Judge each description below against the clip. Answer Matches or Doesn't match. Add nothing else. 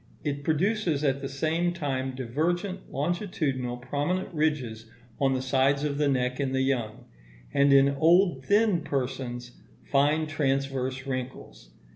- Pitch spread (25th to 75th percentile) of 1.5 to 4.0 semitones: Matches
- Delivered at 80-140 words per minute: Matches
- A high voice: Doesn't match